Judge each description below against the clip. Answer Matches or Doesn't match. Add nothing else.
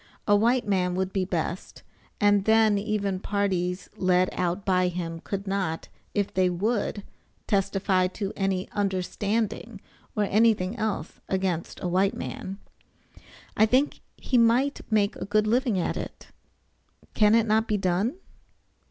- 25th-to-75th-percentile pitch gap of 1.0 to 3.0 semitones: Matches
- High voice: Matches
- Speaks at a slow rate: Doesn't match